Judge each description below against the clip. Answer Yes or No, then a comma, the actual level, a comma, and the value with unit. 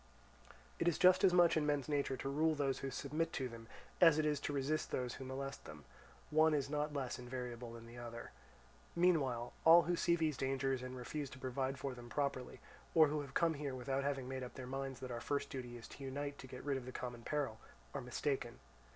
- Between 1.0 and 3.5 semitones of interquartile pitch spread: Yes, average, 2.8 semitones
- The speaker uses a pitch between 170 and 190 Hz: No, low, 135 Hz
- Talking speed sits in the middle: No, fast, 230 wpm